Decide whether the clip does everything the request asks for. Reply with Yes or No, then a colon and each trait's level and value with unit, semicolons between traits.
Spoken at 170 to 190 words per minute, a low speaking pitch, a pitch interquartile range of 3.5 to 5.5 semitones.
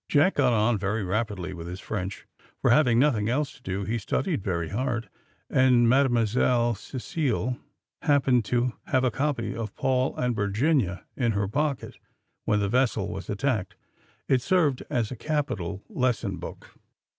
No: average, 155 wpm; low, 120 Hz; average, 4.4 semitones